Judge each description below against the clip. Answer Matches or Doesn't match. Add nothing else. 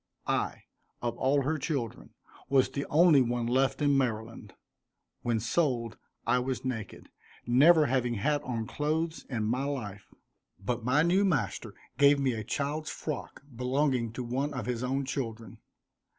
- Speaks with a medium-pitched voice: Doesn't match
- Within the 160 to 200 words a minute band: Doesn't match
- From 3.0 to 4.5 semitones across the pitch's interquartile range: Matches